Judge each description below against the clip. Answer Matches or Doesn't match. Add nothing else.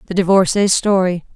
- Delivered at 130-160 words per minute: Matches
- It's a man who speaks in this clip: Doesn't match